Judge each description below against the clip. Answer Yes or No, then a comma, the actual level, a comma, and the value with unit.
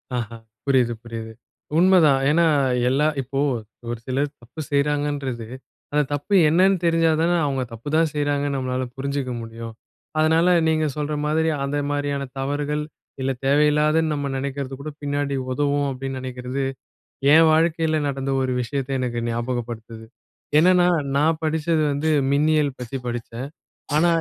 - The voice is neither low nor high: Yes, medium, 145 Hz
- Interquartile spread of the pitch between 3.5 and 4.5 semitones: No, average, 3.1 semitones